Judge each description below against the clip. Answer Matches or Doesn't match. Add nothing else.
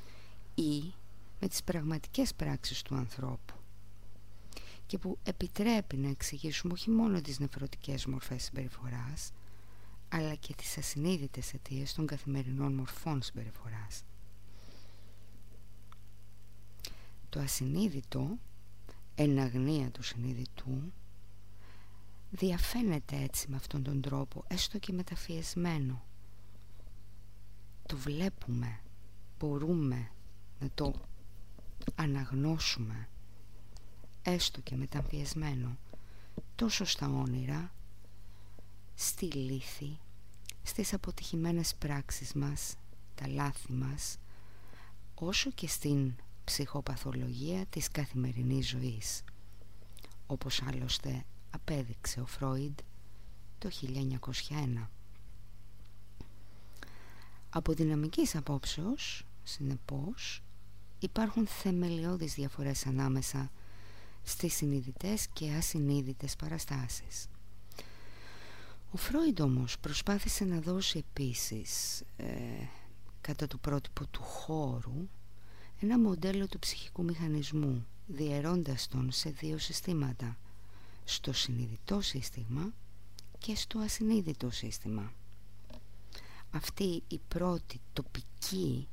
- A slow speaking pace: Matches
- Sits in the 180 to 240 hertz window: Doesn't match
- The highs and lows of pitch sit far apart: Matches